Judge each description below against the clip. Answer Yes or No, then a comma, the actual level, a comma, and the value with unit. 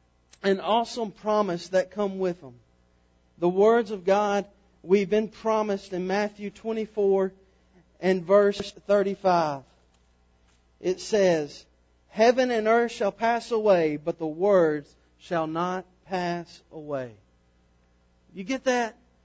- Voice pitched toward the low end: No, medium, 185 Hz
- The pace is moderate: No, slow, 120 wpm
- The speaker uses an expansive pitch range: Yes, wide, 6.1 semitones